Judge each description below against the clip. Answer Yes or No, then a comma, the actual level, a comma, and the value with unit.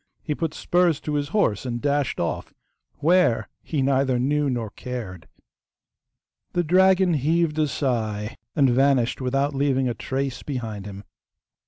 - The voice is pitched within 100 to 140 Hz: Yes, low, 135 Hz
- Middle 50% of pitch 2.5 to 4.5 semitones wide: Yes, average, 3.8 semitones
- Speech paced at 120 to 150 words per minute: Yes, average, 145 wpm